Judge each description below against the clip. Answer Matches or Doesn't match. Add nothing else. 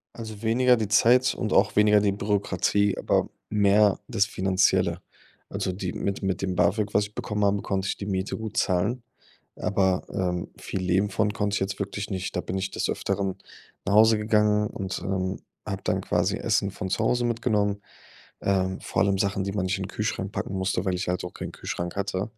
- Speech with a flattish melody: Matches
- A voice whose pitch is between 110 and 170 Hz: Doesn't match